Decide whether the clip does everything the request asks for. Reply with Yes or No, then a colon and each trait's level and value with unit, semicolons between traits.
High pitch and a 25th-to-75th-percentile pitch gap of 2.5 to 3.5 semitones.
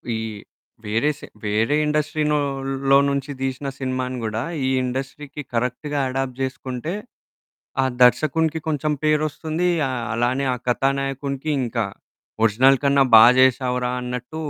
No: low, 135 Hz; average, 2.8 semitones